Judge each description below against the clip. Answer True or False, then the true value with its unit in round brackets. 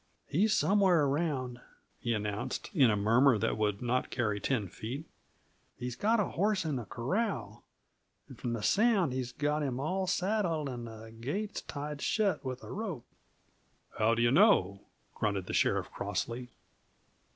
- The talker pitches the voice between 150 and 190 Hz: False (130 Hz)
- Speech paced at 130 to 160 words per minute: True (155 wpm)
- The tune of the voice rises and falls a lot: True (7.7 semitones)